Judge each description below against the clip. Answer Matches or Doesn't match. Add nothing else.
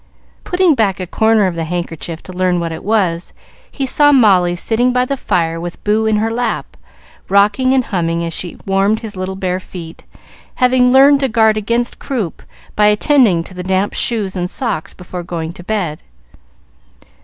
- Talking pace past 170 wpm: Matches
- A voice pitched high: Matches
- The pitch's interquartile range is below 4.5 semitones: Doesn't match